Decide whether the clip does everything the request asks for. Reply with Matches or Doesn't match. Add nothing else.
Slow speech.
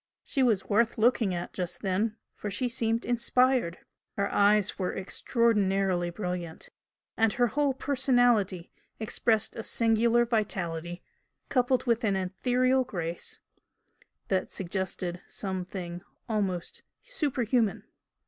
Matches